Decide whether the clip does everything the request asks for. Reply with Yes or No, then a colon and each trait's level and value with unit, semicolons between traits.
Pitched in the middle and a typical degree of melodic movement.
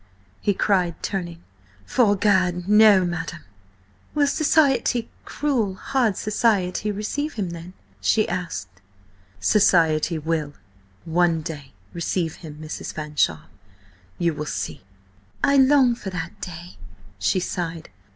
Yes: medium, 180 Hz; average, 4.8 semitones